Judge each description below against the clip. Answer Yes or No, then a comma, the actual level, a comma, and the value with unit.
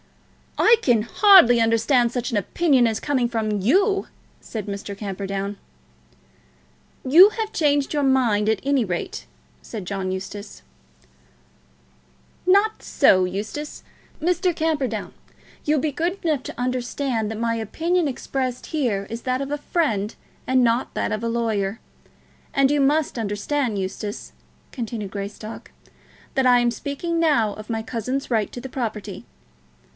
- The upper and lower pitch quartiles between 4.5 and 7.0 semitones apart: Yes, average, 5.3 semitones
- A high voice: Yes, high, 240 Hz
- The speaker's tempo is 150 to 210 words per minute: No, average, 140 wpm